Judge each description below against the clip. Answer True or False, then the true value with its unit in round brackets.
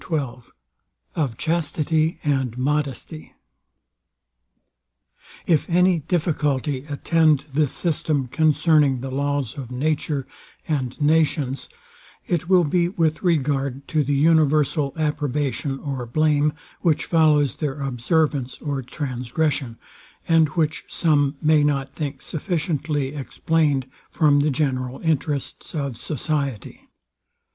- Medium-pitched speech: True (145 Hz)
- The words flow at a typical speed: False (105 wpm)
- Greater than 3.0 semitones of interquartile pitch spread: False (2.5 semitones)